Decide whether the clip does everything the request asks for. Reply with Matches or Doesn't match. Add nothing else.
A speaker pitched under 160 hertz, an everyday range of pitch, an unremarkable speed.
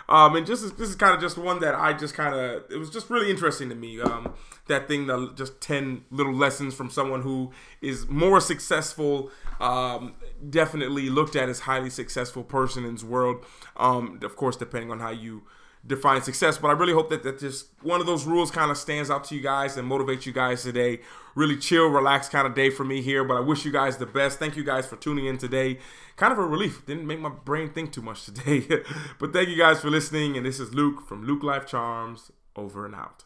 Doesn't match